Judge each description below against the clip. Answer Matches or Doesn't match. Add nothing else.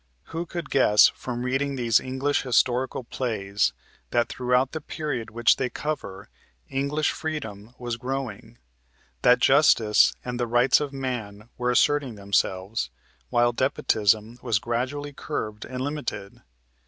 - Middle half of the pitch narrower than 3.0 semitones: Doesn't match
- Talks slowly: Matches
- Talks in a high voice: Doesn't match